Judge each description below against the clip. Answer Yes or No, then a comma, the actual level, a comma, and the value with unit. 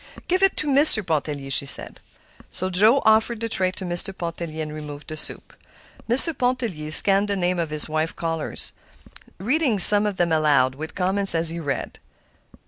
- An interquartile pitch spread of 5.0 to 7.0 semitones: Yes, wide, 5.6 semitones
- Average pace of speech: Yes, average, 175 wpm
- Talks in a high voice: No, medium, 175 Hz